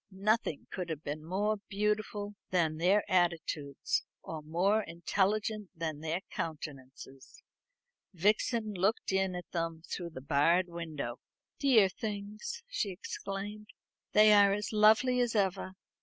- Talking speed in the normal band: No, slow, 125 wpm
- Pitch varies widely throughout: No, average, 4.3 semitones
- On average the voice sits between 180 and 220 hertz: Yes, high, 190 Hz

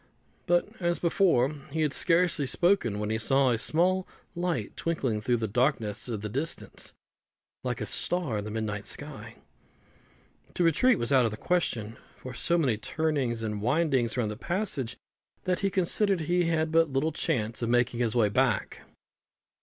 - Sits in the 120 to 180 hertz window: Yes, low, 135 Hz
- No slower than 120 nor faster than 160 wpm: No, average, 175 wpm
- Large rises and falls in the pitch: Yes, wide, 7.1 semitones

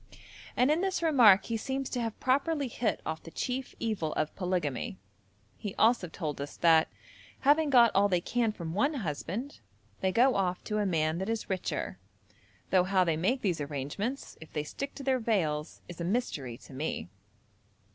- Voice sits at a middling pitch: No, high, 195 Hz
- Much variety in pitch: Yes, wide, 7.5 semitones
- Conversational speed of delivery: Yes, average, 185 wpm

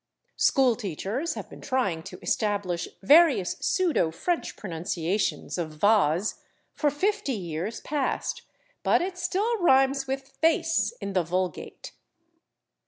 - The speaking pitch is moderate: No, high, 235 Hz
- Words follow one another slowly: Yes, slow, 120 wpm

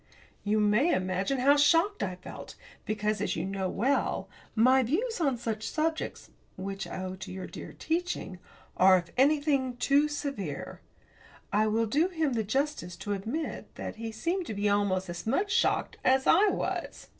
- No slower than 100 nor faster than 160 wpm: No, average, 170 wpm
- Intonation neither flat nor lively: No, wide, 7.0 semitones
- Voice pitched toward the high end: Yes, high, 230 Hz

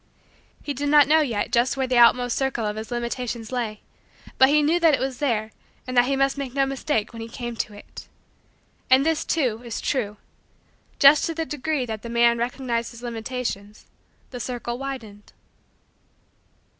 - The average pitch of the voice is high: Yes, high, 245 Hz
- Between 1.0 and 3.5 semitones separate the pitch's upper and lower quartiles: Yes, average, 2.9 semitones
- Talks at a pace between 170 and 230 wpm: Yes, average, 180 wpm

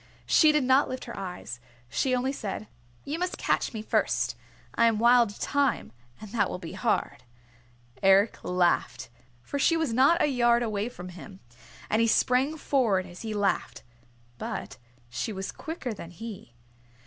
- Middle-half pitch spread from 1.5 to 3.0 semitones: No, wide, 5.4 semitones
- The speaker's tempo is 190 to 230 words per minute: No, average, 165 wpm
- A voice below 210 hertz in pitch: No, high, 230 Hz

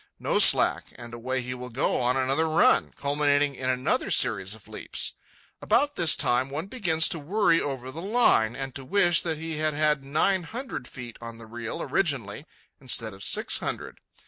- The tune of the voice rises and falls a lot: No, average, 4.5 semitones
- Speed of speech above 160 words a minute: Yes, average, 185 wpm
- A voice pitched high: No, medium, 140 Hz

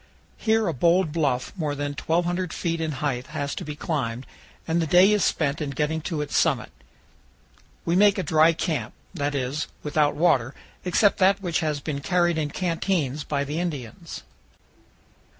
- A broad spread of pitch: No, average, 3.4 semitones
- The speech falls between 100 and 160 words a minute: No, average, 170 wpm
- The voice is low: No, medium, 155 Hz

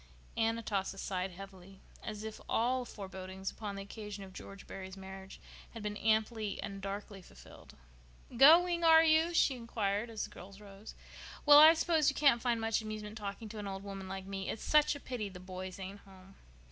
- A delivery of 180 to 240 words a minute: Yes, average, 190 wpm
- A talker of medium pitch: No, high, 210 Hz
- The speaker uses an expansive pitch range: No, average, 3.2 semitones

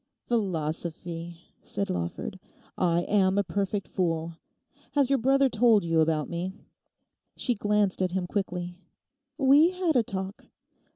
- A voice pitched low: No, high, 190 Hz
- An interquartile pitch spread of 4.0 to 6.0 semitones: Yes, average, 4.8 semitones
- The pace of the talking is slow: Yes, slow, 130 wpm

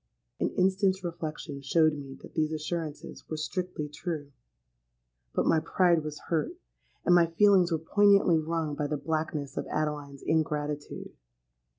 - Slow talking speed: No, average, 145 wpm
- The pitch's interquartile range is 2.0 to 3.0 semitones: Yes, narrow, 2.6 semitones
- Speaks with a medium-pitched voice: Yes, medium, 160 Hz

